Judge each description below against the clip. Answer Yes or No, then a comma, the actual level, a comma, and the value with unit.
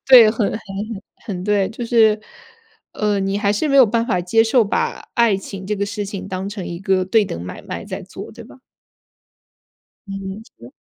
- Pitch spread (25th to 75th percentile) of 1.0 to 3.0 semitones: Yes, narrow, 2.6 semitones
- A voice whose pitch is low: No, high, 205 Hz